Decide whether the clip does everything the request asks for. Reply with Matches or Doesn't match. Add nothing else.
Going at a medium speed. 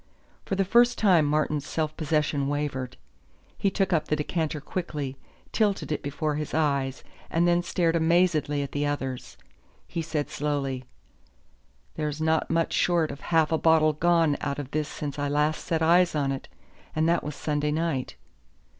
Matches